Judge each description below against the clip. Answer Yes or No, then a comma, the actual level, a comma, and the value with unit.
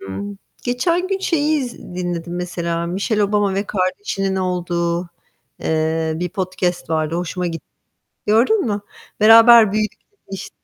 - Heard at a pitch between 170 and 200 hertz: Yes, medium, 185 Hz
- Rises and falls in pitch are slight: No, average, 3.8 semitones